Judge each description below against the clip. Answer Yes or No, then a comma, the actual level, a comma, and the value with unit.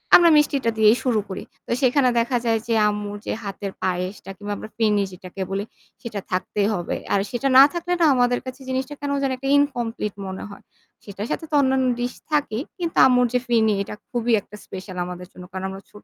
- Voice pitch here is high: Yes, high, 225 Hz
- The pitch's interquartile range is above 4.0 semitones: Yes, average, 4.6 semitones